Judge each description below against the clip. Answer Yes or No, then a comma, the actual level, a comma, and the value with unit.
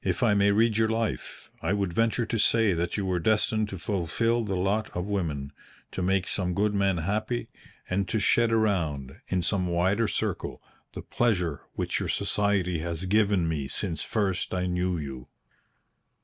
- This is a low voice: Yes, very low, 95 Hz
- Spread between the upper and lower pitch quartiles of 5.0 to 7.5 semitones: No, average, 3.5 semitones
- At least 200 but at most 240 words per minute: No, average, 175 wpm